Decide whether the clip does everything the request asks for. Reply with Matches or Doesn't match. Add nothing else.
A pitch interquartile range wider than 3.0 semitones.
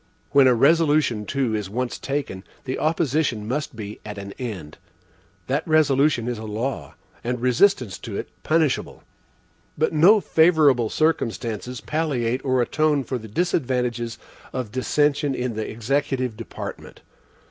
Matches